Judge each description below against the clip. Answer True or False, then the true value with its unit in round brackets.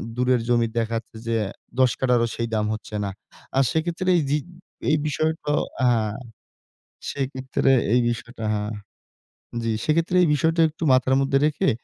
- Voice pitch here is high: False (130 Hz)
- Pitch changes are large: False (4.6 semitones)